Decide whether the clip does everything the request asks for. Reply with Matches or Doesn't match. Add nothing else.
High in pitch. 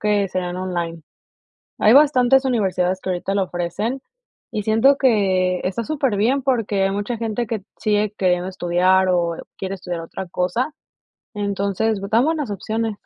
Matches